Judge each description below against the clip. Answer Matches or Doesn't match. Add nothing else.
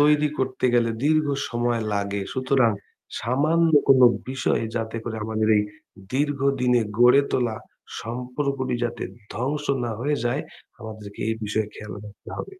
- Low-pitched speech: Matches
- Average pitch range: Matches